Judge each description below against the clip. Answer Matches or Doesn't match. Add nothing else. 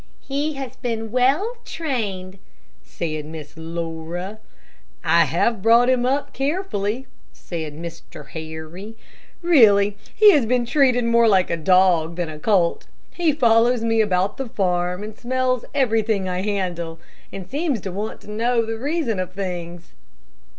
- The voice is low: Doesn't match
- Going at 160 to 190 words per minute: Doesn't match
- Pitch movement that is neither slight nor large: Doesn't match